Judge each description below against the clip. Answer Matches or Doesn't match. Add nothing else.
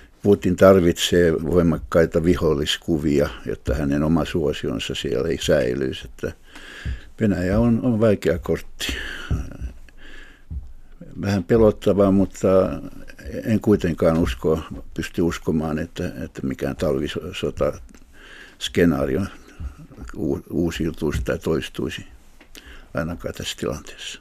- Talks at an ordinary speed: Doesn't match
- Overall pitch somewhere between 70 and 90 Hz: Matches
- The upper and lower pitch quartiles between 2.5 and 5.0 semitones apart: Matches